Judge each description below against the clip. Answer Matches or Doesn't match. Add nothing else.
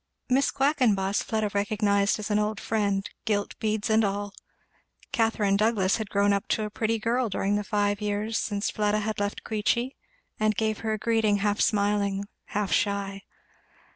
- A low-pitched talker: Doesn't match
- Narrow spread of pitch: Matches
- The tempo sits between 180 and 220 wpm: Doesn't match